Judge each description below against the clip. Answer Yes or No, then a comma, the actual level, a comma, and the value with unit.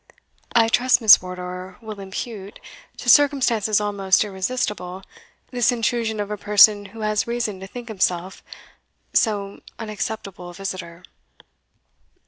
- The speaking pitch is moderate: No, high, 210 Hz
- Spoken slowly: Yes, slow, 120 wpm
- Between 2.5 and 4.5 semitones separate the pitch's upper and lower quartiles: Yes, average, 3.1 semitones